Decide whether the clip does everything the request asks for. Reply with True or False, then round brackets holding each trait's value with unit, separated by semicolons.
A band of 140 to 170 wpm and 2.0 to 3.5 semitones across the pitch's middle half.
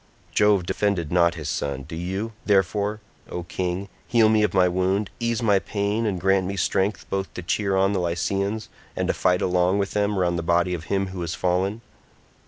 False (200 wpm; 2.5 semitones)